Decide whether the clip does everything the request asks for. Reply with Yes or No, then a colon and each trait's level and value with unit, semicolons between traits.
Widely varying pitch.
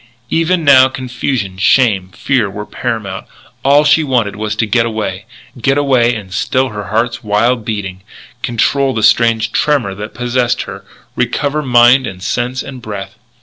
No: average, 3.9 semitones